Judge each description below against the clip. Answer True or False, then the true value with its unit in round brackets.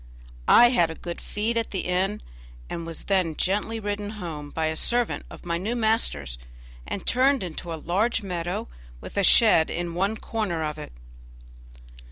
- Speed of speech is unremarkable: True (175 wpm)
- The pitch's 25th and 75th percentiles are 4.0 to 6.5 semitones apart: True (4.7 semitones)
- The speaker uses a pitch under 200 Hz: True (190 Hz)